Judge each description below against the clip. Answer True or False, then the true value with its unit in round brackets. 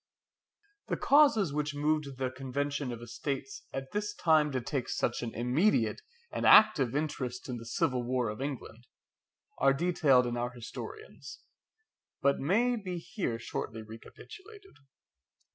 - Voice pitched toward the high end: False (135 Hz)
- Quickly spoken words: False (140 wpm)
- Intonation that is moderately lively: False (5.7 semitones)